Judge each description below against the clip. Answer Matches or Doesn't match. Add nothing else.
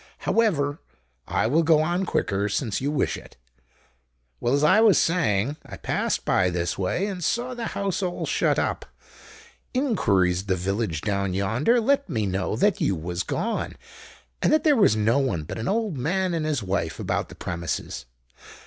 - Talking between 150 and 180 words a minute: Matches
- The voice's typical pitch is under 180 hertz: Matches